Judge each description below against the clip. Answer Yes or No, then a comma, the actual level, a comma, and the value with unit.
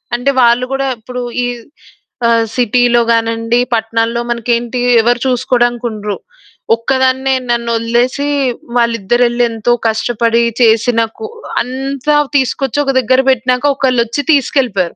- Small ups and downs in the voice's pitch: Yes, narrow, 1.9 semitones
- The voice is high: Yes, high, 240 Hz